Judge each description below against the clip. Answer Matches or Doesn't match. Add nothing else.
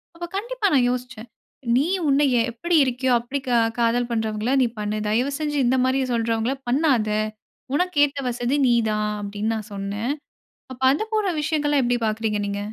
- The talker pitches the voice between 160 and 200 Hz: Doesn't match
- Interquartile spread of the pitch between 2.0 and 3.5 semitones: Doesn't match